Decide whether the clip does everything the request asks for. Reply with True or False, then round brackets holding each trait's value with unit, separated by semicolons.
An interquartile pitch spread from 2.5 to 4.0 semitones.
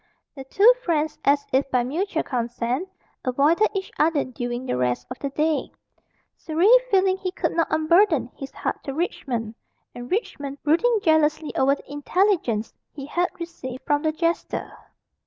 False (4.7 semitones)